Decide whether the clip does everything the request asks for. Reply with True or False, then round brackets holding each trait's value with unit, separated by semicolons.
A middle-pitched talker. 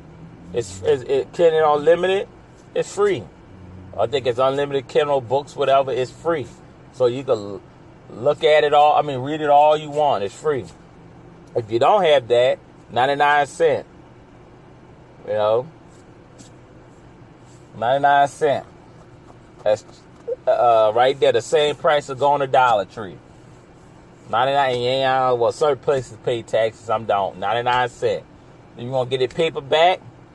True (145 Hz)